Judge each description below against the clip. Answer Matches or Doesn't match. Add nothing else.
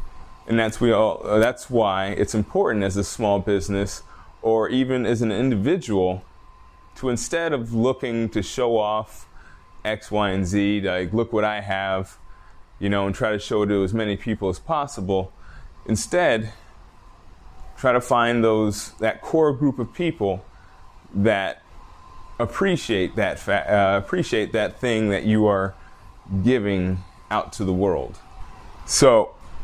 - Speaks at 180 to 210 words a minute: Doesn't match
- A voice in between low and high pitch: Doesn't match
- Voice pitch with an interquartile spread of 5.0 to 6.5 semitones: Doesn't match